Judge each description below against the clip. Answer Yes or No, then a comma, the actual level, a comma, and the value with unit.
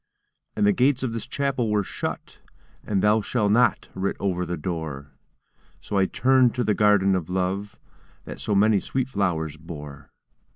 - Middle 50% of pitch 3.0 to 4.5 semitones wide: Yes, average, 4.2 semitones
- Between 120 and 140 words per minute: No, average, 170 wpm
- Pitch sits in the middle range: No, low, 100 Hz